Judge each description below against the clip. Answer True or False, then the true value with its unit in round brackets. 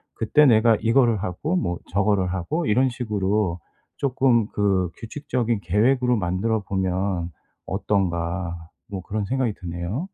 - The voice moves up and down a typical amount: True (4.5 semitones)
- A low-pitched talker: True (105 Hz)